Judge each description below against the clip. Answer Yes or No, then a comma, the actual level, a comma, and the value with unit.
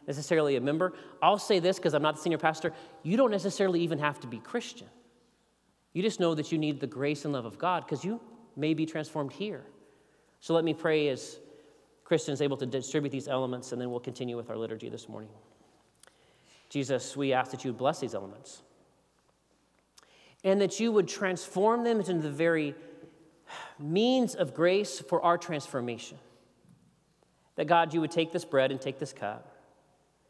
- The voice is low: No, medium, 160 Hz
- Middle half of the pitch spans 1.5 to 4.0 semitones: No, average, 4.8 semitones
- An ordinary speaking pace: Yes, average, 180 wpm